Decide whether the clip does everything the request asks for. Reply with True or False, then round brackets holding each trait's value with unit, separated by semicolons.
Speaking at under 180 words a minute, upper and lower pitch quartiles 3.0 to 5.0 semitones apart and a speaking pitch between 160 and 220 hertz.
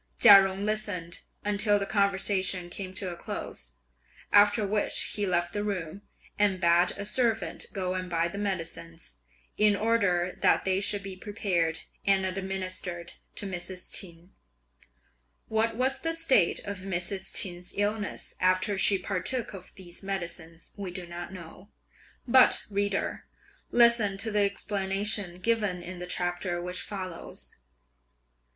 False (140 wpm; 2.5 semitones; 190 Hz)